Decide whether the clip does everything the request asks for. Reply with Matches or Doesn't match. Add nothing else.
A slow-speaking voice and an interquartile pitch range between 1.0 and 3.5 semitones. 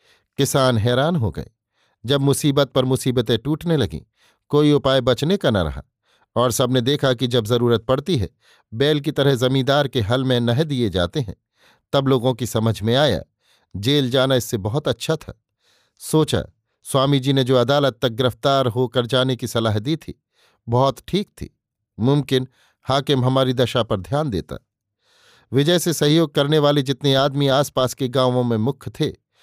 Doesn't match